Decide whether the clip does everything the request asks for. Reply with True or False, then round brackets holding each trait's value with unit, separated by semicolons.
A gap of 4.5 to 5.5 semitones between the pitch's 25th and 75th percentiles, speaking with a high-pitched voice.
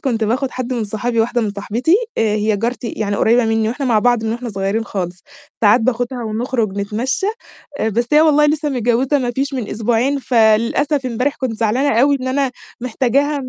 False (3.2 semitones; 240 Hz)